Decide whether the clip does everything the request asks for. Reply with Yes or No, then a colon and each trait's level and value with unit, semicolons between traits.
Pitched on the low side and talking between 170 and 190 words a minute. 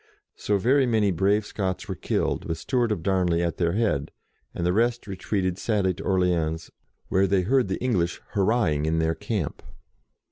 Yes: very low, 95 Hz; average, 175 wpm